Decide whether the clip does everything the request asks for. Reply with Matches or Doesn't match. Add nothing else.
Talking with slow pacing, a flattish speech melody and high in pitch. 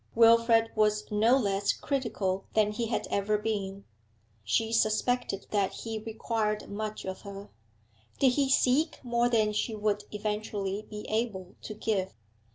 Doesn't match